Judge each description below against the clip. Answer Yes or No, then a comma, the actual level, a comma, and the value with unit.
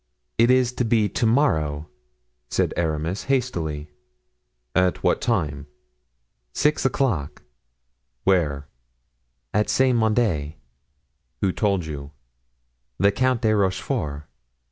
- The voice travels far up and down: Yes, wide, 7.7 semitones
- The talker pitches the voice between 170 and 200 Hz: No, very low, 95 Hz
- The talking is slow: Yes, slow, 100 wpm